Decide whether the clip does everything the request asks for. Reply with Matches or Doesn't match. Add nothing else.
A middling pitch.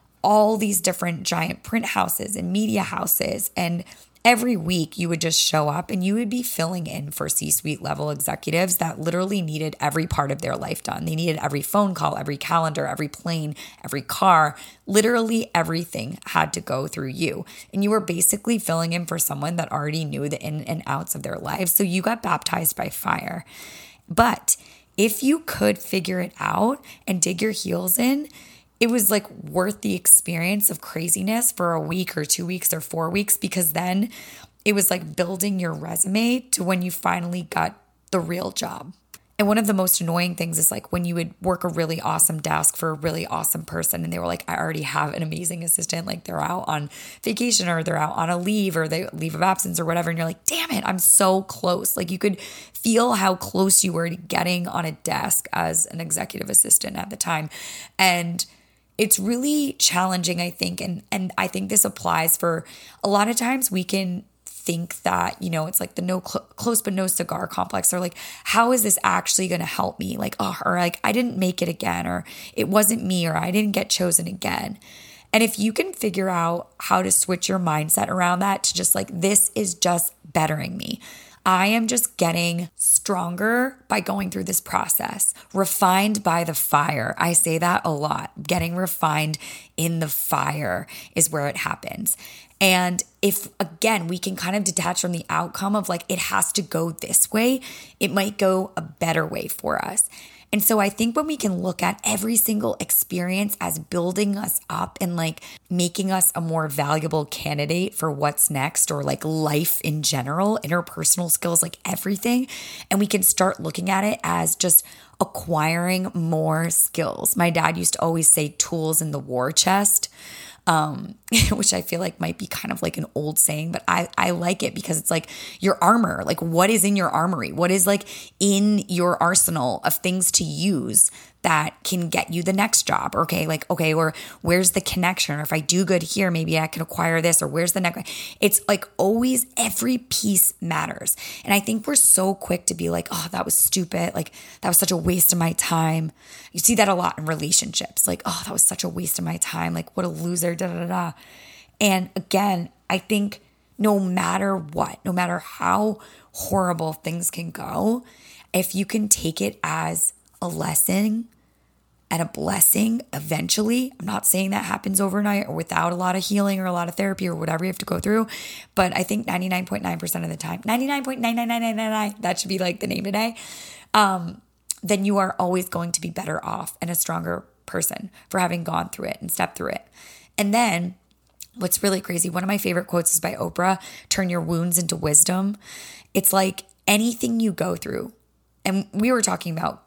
Matches